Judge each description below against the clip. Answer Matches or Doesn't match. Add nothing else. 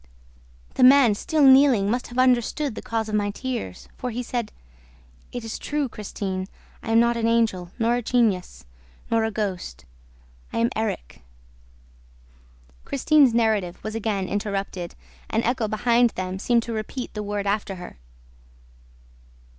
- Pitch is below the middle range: Doesn't match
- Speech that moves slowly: Doesn't match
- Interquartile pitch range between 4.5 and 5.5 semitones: Doesn't match